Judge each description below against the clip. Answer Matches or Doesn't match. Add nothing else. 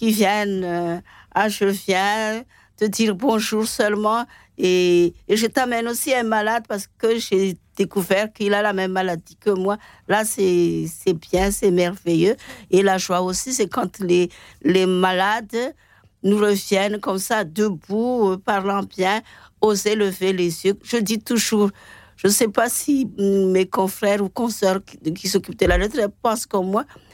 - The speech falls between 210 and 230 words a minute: Doesn't match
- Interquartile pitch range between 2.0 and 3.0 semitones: Matches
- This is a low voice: Doesn't match